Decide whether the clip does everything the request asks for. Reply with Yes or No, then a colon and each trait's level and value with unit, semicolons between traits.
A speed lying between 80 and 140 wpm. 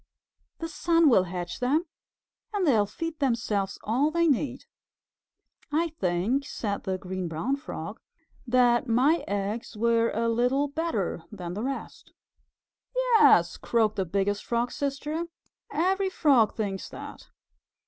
Yes: slow, 135 wpm